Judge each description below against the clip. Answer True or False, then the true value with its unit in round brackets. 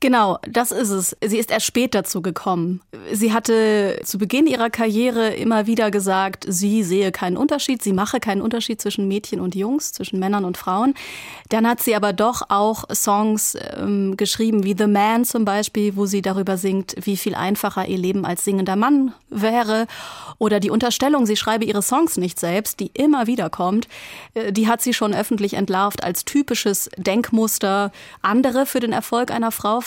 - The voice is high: True (215 Hz)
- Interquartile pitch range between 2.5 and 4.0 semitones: True (2.9 semitones)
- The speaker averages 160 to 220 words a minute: True (180 wpm)